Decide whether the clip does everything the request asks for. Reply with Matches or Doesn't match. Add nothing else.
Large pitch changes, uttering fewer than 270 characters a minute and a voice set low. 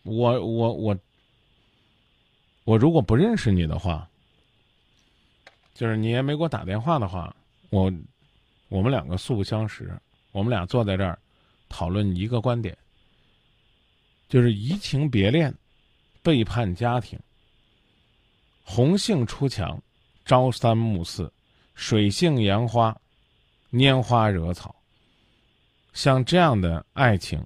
Doesn't match